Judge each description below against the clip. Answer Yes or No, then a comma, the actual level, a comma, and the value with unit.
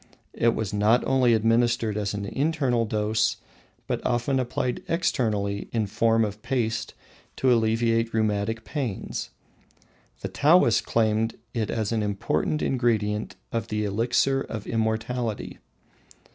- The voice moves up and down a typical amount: No, narrow, 2.1 semitones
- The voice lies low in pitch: Yes, low, 115 Hz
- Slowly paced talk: Yes, slow, 125 wpm